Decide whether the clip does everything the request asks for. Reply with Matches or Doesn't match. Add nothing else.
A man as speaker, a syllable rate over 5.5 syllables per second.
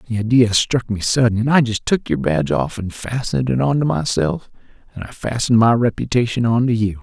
Matches